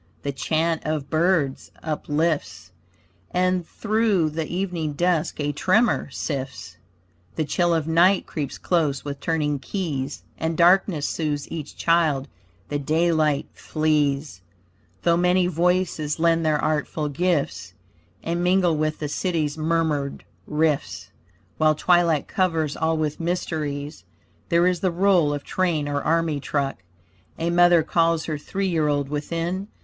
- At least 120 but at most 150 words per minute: Yes, slow, 135 wpm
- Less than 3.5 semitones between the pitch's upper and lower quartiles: Yes, average, 2.9 semitones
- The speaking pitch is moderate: Yes, medium, 160 Hz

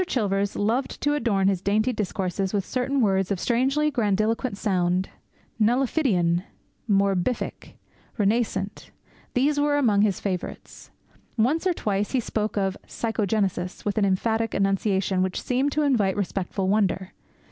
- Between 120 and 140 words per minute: Yes, slow, 135 wpm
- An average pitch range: Yes, average, 4.1 semitones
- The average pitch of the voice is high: Yes, high, 205 Hz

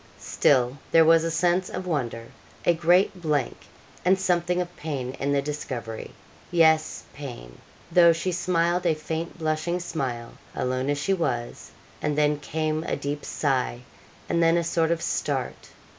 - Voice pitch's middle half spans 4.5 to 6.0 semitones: No, average, 3.6 semitones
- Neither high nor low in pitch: Yes, medium, 160 Hz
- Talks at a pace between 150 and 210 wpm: Yes, average, 160 wpm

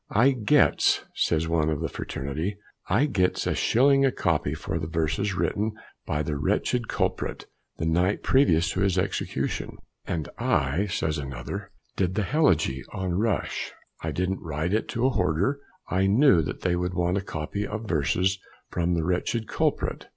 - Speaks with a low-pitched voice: Yes, very low, 90 Hz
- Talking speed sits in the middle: Yes, average, 165 wpm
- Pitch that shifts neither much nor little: Yes, average, 4.6 semitones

